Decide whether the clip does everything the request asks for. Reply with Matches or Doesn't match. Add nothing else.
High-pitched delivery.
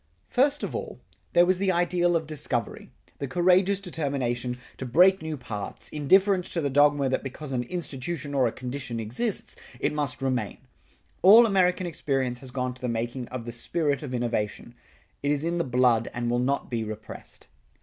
Doesn't match